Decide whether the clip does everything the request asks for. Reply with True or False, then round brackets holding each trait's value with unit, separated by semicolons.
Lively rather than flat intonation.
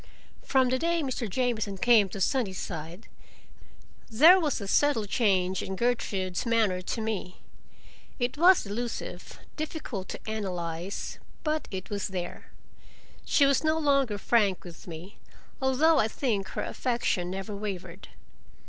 True (5.7 semitones)